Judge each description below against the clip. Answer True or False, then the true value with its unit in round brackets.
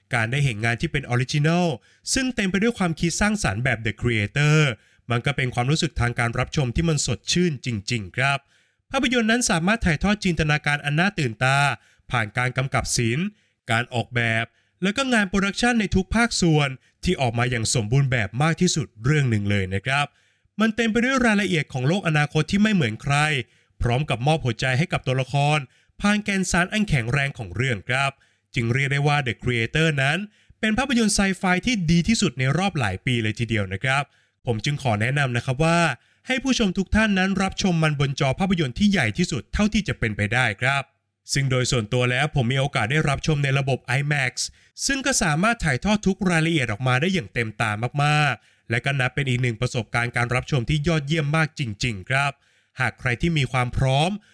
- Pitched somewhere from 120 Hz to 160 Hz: True (140 Hz)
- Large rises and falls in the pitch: True (6.3 semitones)